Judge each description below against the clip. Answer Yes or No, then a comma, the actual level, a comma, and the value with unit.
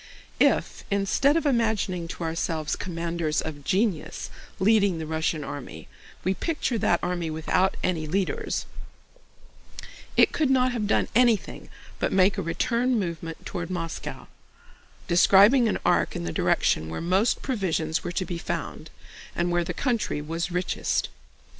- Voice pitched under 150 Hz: No, medium, 180 Hz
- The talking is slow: No, average, 145 wpm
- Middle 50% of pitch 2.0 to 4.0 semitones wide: No, average, 4.6 semitones